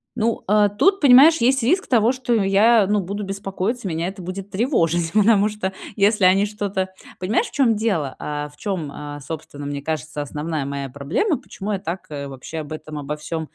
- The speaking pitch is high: Yes, high, 195 Hz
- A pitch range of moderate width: No, wide, 5.8 semitones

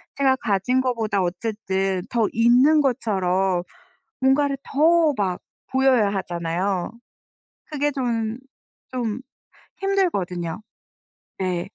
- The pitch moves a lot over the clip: Yes, wide, 5.8 semitones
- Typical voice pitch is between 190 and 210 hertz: No, high, 225 Hz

